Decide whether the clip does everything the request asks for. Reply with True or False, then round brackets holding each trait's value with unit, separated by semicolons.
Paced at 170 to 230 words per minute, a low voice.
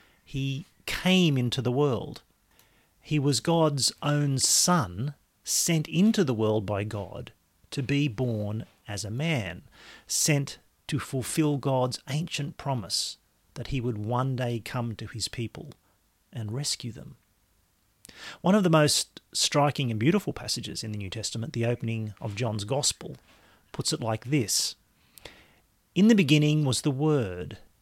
False (145 wpm; 125 Hz)